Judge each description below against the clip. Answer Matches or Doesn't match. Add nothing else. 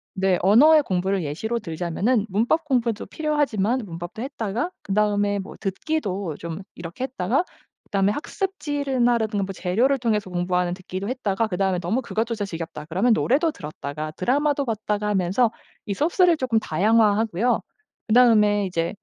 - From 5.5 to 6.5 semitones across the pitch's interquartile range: Doesn't match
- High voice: Matches